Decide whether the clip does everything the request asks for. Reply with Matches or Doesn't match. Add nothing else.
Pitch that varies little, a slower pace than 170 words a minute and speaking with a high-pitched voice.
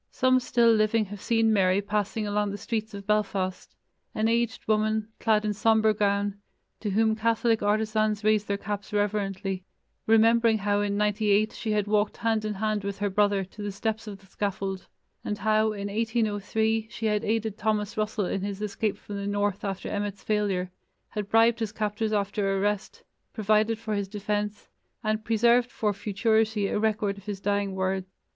Doesn't match